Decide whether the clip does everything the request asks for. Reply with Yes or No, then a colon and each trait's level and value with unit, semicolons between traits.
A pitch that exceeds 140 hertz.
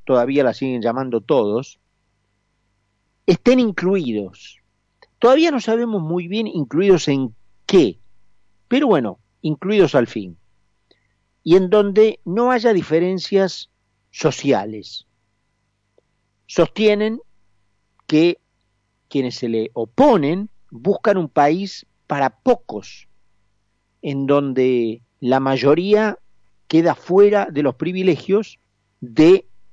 No: low, 135 Hz